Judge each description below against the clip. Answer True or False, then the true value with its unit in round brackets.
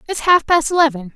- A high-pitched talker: True (300 Hz)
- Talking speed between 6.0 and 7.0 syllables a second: True (6.2 syllables/s)